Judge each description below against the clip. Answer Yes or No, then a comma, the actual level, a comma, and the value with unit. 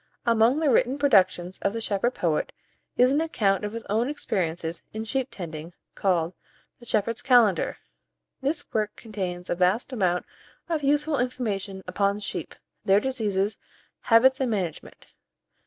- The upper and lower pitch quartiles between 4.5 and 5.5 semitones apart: Yes, average, 5.1 semitones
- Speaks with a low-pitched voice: No, high, 215 Hz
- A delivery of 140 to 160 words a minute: Yes, average, 145 wpm